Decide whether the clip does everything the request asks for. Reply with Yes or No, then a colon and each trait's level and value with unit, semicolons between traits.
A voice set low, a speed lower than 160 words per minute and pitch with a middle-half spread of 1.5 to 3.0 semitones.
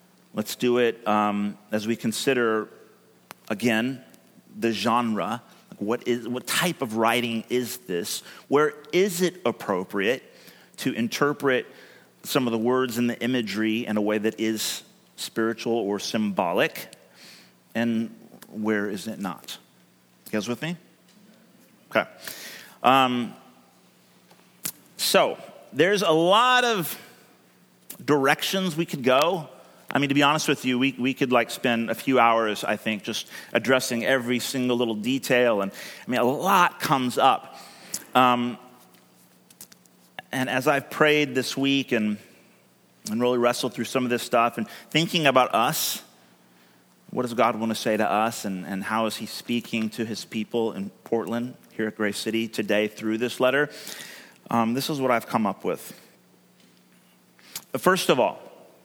No: low, 120 Hz; average, 150 wpm; average, 3.5 semitones